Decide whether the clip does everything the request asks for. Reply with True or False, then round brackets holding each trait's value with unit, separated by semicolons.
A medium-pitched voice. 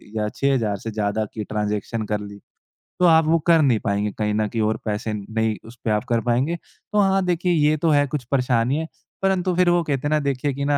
False (125 Hz)